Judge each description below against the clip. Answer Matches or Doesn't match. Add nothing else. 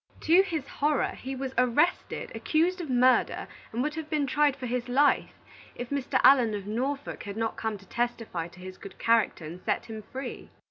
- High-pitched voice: Matches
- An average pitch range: Matches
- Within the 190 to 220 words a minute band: Matches